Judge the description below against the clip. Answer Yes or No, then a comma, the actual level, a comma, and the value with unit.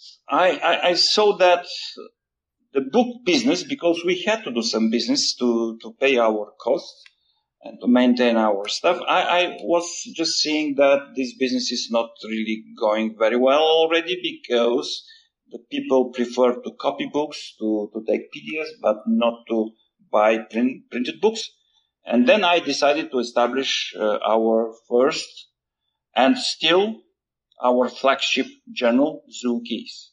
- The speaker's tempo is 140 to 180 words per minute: Yes, average, 145 wpm